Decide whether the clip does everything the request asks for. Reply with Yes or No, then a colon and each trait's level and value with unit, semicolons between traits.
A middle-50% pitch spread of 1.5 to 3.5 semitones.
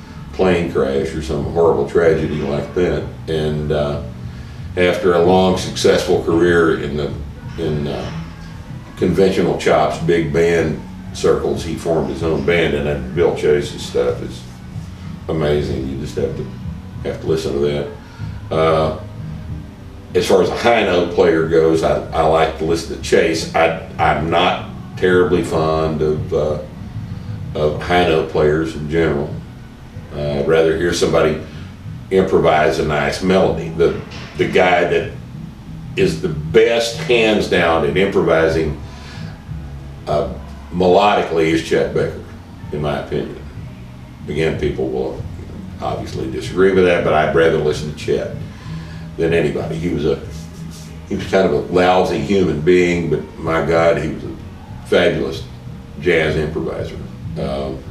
Yes: average, 3.1 semitones